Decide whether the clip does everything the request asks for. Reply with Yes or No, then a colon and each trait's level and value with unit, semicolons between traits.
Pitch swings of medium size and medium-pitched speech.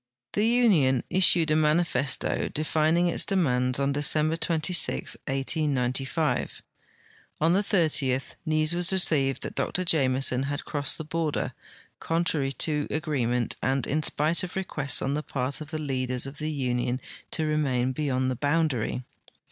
Yes: average, 3.4 semitones; medium, 150 Hz